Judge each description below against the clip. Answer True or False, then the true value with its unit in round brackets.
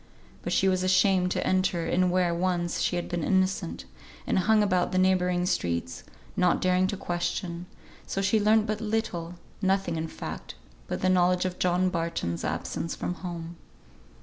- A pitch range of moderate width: False (1.5 semitones)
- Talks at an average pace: True (170 wpm)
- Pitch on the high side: False (180 Hz)